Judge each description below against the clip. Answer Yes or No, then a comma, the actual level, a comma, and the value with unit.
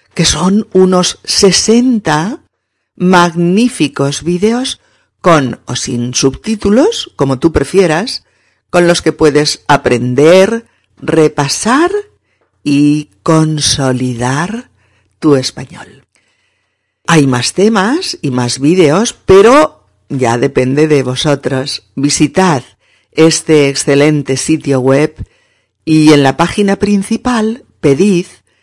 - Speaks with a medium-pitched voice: Yes, medium, 155 Hz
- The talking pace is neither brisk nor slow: No, slow, 95 wpm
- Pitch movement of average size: No, wide, 6.4 semitones